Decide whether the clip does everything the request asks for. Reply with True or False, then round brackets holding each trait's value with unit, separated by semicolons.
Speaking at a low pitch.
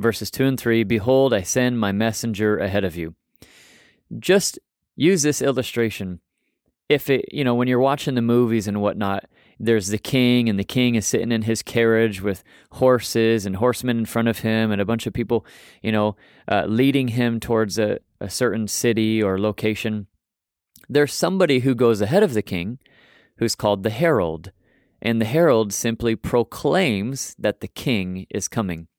True (115 Hz)